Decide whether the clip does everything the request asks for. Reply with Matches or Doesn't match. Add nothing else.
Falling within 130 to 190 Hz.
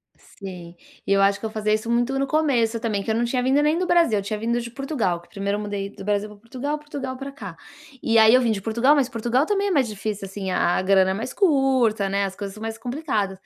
Doesn't match